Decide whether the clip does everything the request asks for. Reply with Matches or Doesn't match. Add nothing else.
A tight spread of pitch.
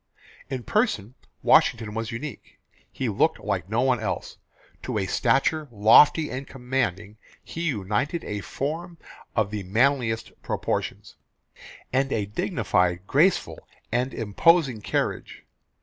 Doesn't match